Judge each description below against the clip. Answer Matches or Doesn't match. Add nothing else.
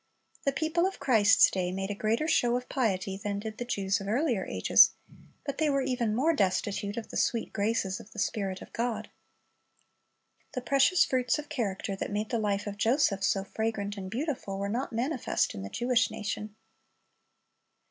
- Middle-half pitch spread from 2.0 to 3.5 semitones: Doesn't match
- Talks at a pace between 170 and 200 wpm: Matches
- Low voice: Doesn't match